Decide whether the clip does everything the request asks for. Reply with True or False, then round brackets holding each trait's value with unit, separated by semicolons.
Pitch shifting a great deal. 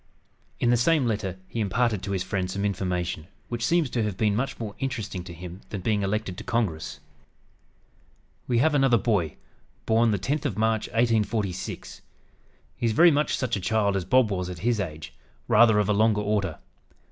False (3.7 semitones)